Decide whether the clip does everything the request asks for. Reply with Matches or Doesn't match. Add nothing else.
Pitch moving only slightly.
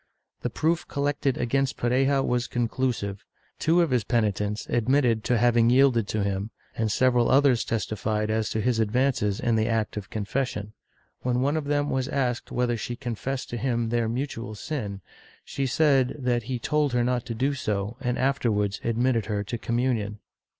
Doesn't match